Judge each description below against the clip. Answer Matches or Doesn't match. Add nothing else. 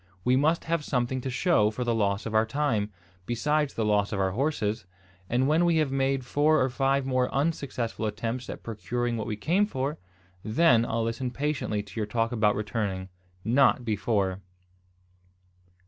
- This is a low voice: Matches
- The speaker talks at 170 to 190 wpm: Matches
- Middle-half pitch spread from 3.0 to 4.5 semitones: Matches